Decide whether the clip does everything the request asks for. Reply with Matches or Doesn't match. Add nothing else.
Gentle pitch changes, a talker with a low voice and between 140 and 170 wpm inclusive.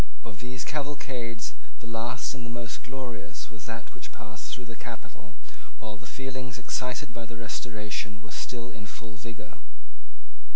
Matches